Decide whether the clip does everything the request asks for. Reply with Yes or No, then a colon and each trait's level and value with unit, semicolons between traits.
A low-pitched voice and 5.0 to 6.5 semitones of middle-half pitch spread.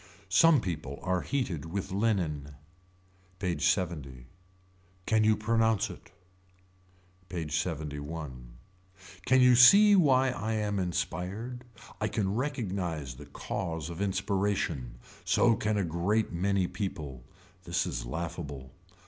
Yes: very low, 95 Hz; wide, 5.4 semitones